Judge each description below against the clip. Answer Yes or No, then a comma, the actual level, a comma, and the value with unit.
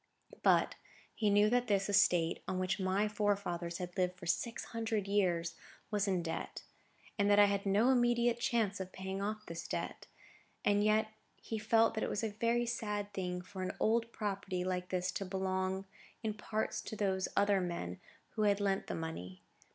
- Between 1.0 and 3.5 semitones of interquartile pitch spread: Yes, narrow, 2.5 semitones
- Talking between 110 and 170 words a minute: No, average, 180 wpm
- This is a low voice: No, high, 200 Hz